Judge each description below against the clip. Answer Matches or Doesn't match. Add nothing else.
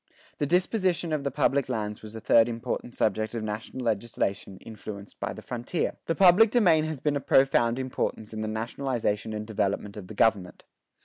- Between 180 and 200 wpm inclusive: Matches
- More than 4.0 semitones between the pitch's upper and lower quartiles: Matches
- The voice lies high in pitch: Doesn't match